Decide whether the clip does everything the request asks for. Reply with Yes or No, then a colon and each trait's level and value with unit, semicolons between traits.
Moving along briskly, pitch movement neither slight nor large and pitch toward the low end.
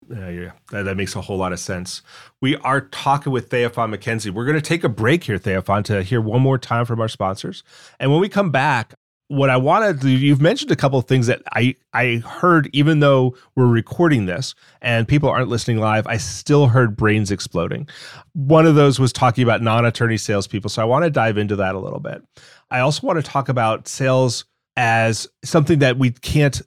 Yes: fast, 220 wpm; average, 4.1 semitones; low, 125 Hz